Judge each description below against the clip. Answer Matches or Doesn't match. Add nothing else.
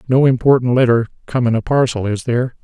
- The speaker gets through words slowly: Doesn't match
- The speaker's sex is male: Matches